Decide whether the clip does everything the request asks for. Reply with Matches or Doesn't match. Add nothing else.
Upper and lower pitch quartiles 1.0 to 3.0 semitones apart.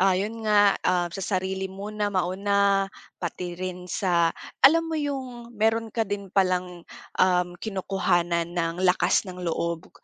Matches